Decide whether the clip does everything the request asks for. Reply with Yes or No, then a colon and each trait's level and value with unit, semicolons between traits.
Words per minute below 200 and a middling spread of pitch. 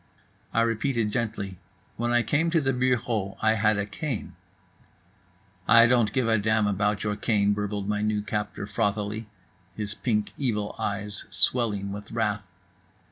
No: average, 150 wpm; narrow, 2.3 semitones